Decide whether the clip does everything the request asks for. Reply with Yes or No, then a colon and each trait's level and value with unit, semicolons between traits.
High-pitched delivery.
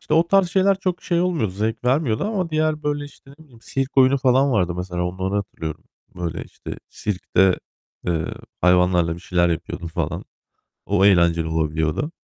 No: low, 105 Hz